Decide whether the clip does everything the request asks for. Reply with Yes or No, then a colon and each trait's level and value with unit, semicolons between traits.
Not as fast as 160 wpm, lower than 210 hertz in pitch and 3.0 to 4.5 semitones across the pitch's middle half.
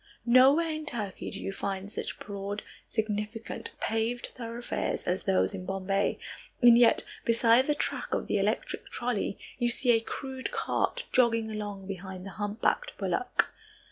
No: average, 150 wpm; high, 225 Hz; average, 3.6 semitones